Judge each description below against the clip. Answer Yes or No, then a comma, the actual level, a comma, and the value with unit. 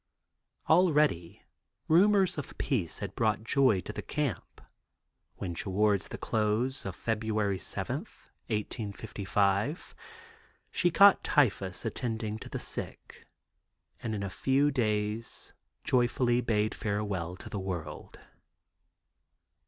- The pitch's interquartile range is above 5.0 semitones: No, average, 4.6 semitones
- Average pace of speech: No, slow, 105 wpm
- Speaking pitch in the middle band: No, low, 110 Hz